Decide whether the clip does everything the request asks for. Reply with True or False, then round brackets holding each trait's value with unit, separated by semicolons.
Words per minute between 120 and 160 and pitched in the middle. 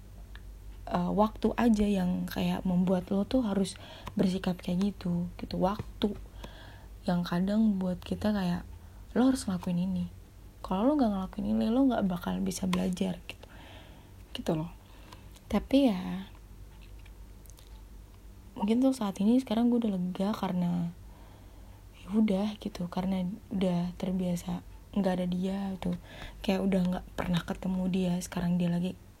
True (135 wpm; 180 Hz)